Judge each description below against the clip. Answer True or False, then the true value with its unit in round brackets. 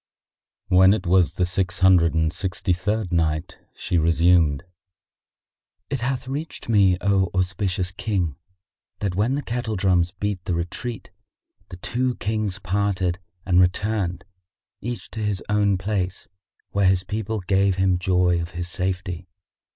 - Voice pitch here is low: True (95 Hz)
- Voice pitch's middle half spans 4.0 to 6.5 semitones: False (2.6 semitones)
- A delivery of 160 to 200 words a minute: False (145 wpm)